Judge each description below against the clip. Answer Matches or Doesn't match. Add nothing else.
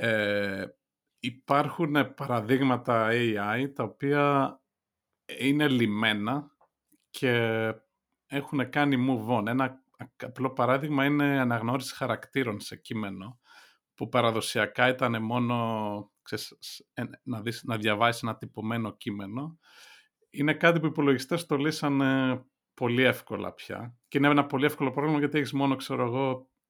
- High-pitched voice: Doesn't match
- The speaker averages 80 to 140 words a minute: Matches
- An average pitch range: Matches